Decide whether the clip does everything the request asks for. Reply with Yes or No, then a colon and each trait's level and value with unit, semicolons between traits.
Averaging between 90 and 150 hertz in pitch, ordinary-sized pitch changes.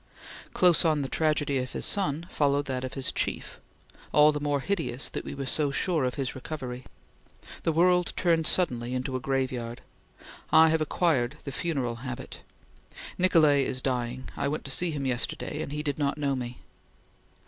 Yes: medium, 140 Hz; average, 3.4 semitones